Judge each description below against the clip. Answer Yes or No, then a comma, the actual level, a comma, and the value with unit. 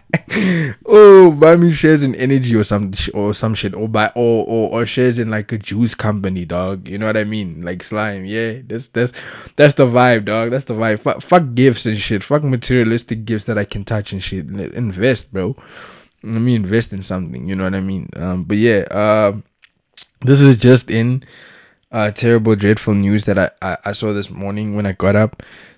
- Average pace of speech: No, fast, 210 wpm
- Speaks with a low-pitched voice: Yes, low, 110 Hz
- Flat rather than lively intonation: No, average, 3.3 semitones